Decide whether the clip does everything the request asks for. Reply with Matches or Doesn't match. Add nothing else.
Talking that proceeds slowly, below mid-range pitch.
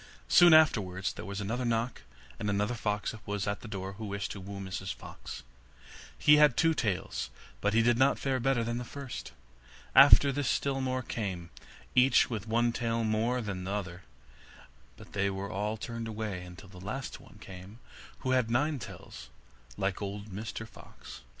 Doesn't match